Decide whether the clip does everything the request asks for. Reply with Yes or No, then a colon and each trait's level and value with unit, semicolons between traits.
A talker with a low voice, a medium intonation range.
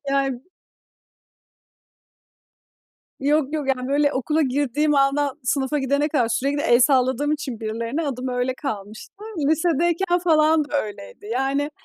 No: very high, 275 Hz; average, 3.0 semitones